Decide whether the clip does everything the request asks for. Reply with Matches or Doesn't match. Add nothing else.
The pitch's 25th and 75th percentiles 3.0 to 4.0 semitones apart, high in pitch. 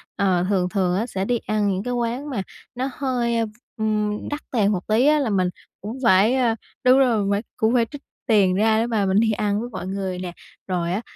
Matches